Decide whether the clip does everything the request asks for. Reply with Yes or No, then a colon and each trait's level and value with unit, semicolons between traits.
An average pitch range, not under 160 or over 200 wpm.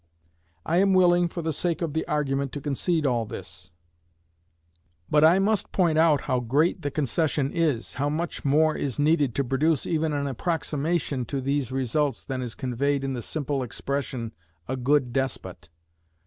Yes: average, 3.3 semitones; average, 170 wpm